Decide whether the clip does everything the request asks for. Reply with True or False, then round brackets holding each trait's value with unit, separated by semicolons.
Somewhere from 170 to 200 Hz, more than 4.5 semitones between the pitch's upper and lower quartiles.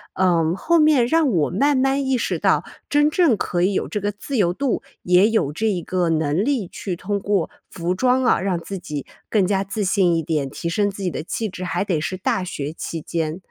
True (190 Hz; 5.1 semitones)